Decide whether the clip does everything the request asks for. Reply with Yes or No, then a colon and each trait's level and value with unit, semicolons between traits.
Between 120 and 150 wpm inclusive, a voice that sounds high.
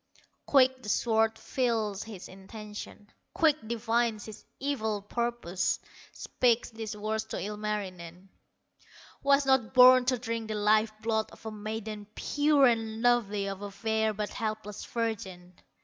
Yes: slow, 135 wpm; high, 220 Hz